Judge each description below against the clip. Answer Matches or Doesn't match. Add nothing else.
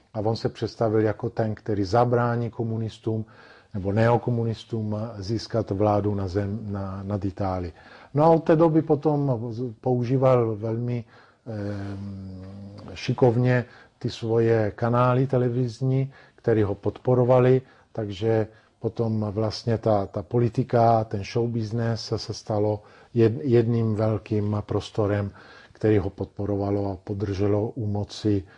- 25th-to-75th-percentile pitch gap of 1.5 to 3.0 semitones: Matches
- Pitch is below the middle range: Matches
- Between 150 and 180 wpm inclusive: Doesn't match